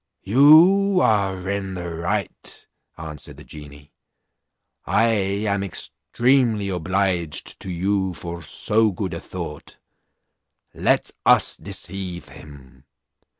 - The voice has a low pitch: Yes, very low, 95 Hz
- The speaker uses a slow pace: Yes, slow, 105 wpm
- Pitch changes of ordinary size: Yes, average, 3.7 semitones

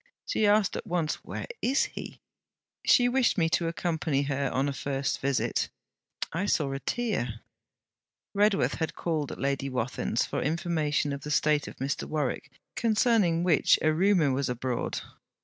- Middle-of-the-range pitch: Yes, medium, 155 Hz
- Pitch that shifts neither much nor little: Yes, average, 4.9 semitones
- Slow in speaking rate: No, average, 160 wpm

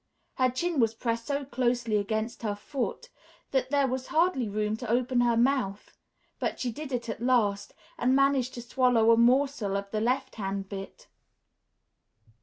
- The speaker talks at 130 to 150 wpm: No, average, 170 wpm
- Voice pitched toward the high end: Yes, high, 240 Hz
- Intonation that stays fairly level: No, average, 3.2 semitones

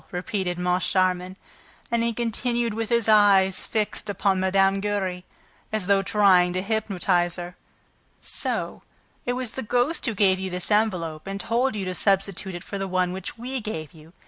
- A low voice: No, high, 195 Hz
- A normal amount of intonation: Yes, average, 3.1 semitones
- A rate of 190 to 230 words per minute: No, average, 170 wpm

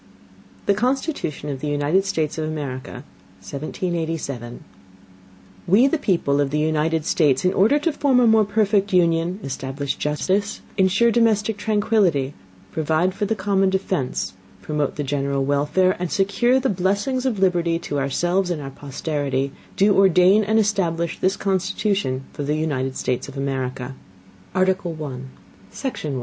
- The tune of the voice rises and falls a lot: Yes, wide, 5.8 semitones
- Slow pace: No, average, 150 wpm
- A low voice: No, medium, 170 Hz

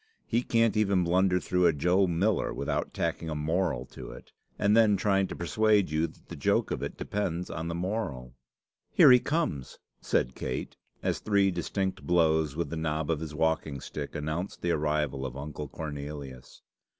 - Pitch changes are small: No, average, 4.5 semitones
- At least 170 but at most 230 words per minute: Yes, average, 180 wpm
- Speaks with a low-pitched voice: Yes, very low, 85 Hz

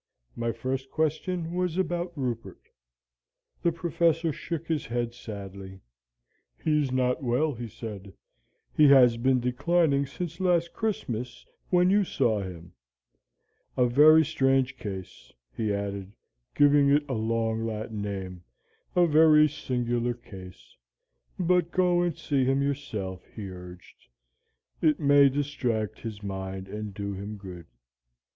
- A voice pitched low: Yes, low, 125 Hz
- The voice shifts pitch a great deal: Yes, wide, 6.8 semitones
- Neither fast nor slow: No, slow, 130 wpm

